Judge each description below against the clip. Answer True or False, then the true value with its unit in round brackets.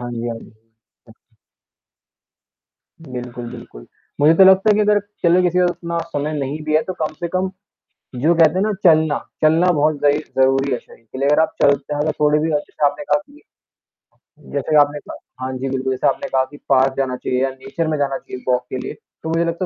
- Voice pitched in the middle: True (150 Hz)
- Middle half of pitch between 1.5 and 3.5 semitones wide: False (4.1 semitones)